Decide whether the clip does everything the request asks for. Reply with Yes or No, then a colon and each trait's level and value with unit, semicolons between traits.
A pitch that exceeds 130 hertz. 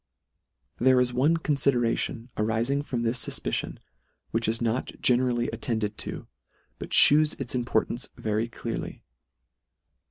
No: low, 120 Hz